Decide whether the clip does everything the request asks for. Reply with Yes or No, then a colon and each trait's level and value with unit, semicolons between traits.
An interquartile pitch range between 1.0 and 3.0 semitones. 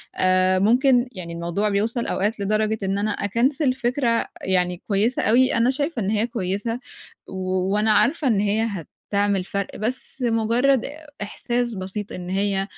No: average, 3.7 semitones